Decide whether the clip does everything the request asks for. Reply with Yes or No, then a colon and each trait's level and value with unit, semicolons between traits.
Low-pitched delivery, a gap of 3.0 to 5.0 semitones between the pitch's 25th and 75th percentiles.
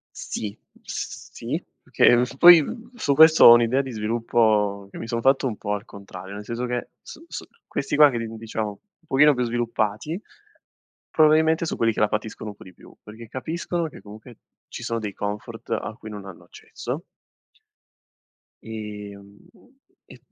Yes: low, 115 Hz; average, 4.5 semitones